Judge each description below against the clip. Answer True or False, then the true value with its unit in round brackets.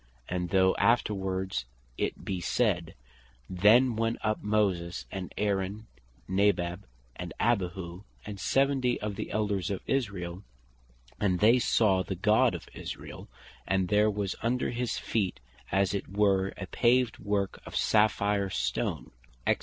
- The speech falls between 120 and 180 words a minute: True (145 wpm)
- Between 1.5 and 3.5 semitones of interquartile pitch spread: True (2.5 semitones)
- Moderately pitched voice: False (100 Hz)